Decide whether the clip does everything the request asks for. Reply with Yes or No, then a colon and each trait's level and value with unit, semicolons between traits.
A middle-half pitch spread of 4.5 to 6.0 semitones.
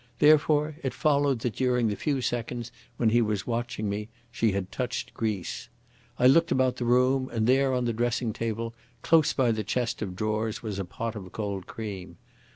No: average, 3.1 semitones